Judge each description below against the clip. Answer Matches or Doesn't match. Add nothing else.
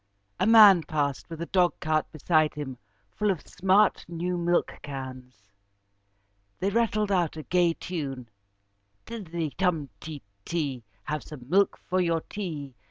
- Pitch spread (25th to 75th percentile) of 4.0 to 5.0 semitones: Matches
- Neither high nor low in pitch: Matches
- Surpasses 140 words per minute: Doesn't match